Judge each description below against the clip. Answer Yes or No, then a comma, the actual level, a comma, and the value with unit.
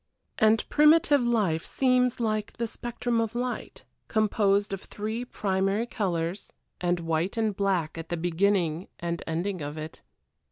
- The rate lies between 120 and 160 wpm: Yes, average, 145 wpm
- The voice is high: Yes, high, 200 Hz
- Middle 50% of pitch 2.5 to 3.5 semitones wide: No, average, 5.0 semitones